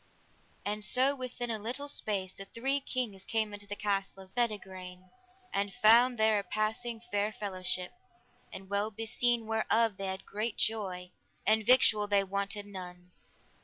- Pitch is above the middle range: Yes, high, 210 Hz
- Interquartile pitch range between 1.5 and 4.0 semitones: Yes, average, 2.7 semitones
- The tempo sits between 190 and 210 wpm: No, average, 155 wpm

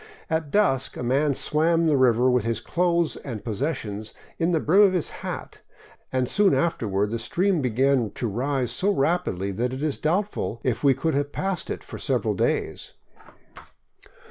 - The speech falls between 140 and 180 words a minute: Yes, average, 175 wpm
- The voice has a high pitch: No, medium, 140 Hz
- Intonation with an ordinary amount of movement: No, wide, 5.8 semitones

